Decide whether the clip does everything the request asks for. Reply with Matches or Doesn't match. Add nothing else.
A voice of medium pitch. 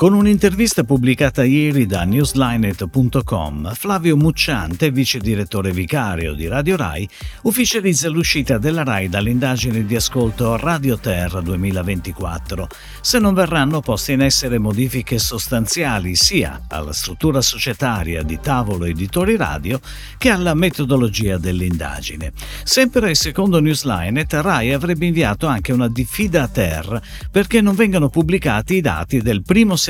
Doesn't match